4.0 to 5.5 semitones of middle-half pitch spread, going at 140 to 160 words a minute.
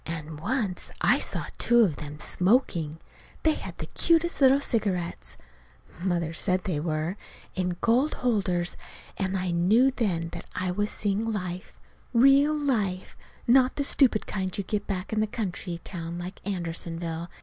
Yes: average, 5.2 semitones; average, 155 wpm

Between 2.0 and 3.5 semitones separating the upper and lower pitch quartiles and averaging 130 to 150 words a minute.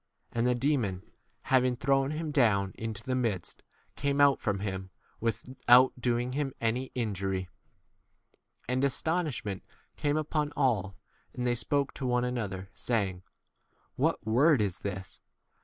No: average, 5.1 semitones; average, 140 wpm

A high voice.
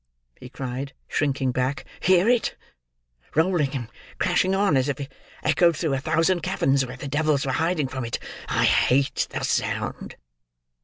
No: medium, 140 Hz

